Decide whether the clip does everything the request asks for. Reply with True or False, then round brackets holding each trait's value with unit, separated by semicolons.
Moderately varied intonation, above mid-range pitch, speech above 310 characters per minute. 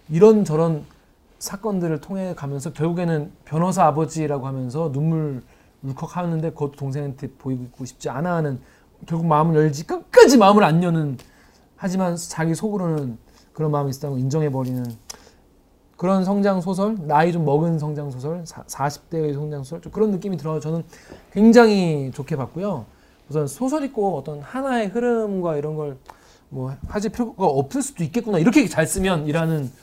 False (4.8 semitones; 160 Hz; 335 characters per minute)